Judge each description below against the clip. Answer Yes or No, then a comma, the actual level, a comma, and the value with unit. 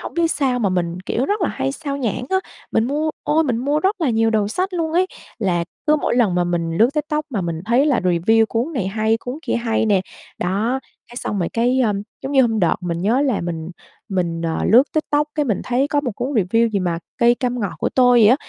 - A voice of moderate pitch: No, high, 235 Hz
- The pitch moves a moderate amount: No, wide, 6.6 semitones